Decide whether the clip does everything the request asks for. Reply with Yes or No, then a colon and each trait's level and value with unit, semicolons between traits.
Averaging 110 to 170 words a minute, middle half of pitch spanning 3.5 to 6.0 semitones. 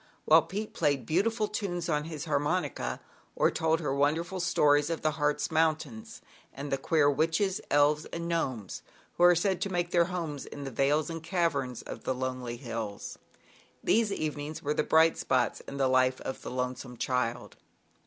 No: average, 180 wpm; average, 4.2 semitones